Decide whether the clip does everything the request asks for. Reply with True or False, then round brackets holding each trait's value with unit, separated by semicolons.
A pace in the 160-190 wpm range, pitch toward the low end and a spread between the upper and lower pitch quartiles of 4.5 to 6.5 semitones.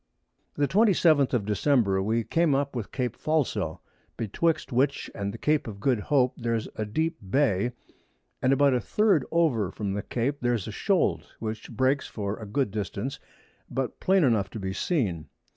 True (175 wpm; 125 Hz; 5.3 semitones)